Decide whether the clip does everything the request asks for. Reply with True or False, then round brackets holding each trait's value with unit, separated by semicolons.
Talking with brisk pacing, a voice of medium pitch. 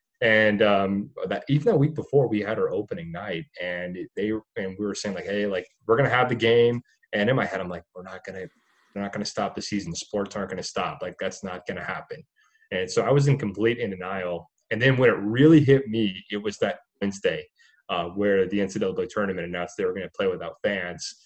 False (230 wpm; 110 Hz)